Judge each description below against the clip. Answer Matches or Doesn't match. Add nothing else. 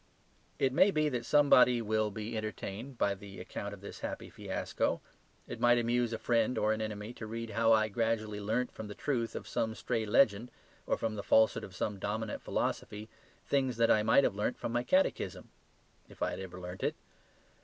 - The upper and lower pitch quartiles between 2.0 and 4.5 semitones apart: Matches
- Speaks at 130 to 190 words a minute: Doesn't match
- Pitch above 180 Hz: Doesn't match